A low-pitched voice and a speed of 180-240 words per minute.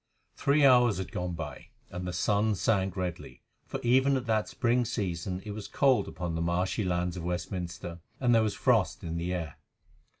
Yes: very low, 95 Hz; average, 190 wpm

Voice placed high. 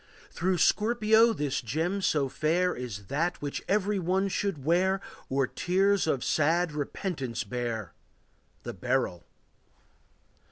No: medium, 165 Hz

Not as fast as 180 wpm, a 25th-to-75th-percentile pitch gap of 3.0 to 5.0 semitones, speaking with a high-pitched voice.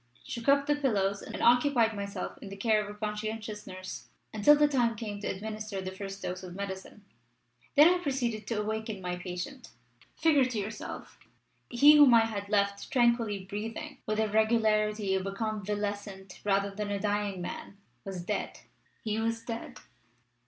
No: average, 170 wpm; narrow, 2.5 semitones; high, 215 Hz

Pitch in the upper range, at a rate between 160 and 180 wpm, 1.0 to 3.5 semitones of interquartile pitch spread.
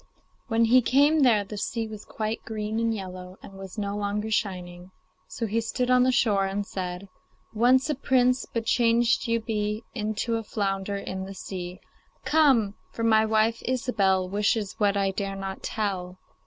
Yes: high, 215 Hz; average, 175 wpm; average, 2.9 semitones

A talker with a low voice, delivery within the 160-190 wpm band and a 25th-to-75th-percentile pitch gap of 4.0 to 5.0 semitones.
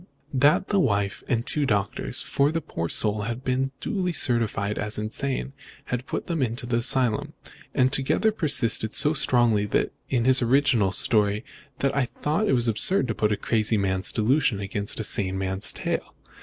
Yes: low, 120 Hz; average, 175 wpm; average, 4.5 semitones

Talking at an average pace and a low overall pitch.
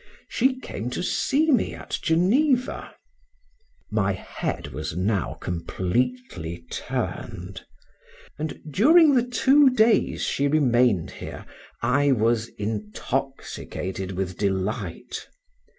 No: slow, 100 wpm; low, 120 Hz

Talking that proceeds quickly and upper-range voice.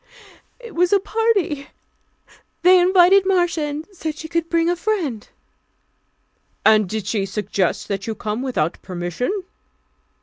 No: slow, 135 wpm; very high, 320 Hz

